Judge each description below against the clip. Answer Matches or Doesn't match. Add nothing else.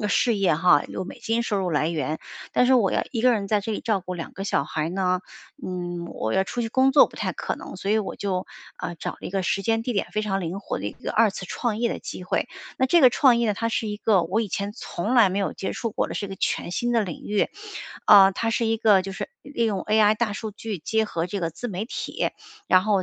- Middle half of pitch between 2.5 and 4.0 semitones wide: Matches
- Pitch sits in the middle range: Doesn't match